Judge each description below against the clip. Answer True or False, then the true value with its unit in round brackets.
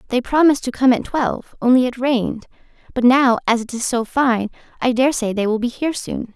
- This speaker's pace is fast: True (225 wpm)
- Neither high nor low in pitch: False (245 Hz)